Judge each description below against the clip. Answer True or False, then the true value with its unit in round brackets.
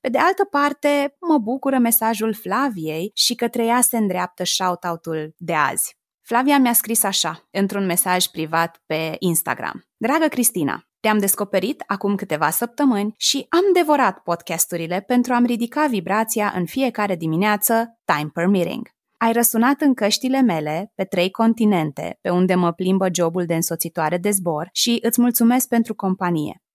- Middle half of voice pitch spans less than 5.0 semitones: False (5.5 semitones)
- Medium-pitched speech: False (205 Hz)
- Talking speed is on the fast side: False (155 wpm)